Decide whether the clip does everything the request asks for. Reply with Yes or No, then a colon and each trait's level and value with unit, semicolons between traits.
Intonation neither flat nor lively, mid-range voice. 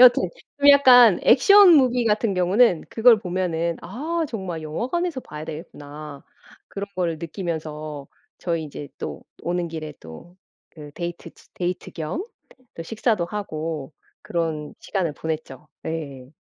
No: wide, 6.4 semitones; medium, 170 Hz